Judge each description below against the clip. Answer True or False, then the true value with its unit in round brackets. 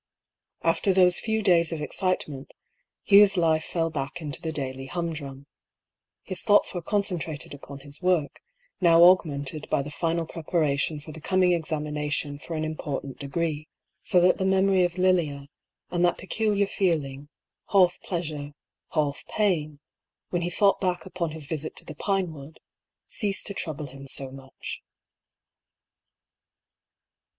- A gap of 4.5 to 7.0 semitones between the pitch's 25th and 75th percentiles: False (3.8 semitones)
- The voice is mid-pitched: True (165 Hz)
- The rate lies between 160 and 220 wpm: False (150 wpm)